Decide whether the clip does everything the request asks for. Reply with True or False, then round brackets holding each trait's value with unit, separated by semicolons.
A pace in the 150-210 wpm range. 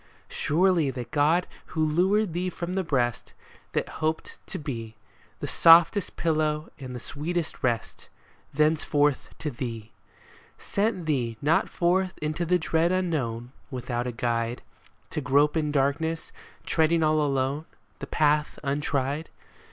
False (135 wpm)